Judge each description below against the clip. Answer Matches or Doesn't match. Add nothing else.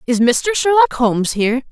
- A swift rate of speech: Doesn't match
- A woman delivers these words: Matches